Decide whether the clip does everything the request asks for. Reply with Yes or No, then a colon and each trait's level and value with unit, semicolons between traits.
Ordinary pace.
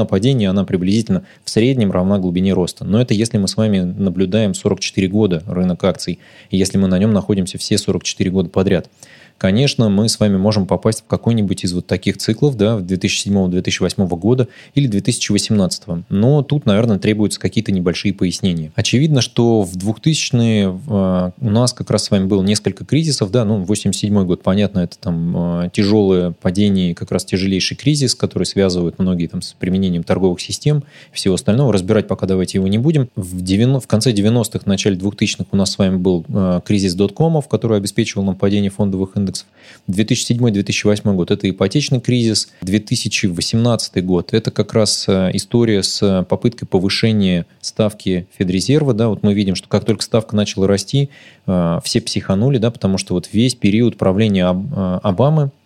No: fast, 165 wpm